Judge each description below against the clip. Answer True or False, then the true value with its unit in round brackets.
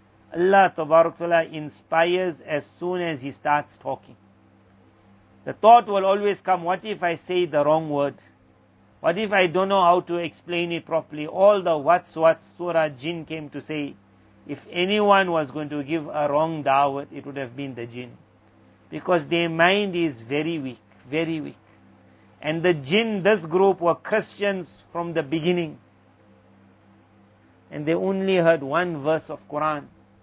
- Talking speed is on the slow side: False (160 wpm)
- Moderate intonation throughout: True (4.4 semitones)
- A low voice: False (160 Hz)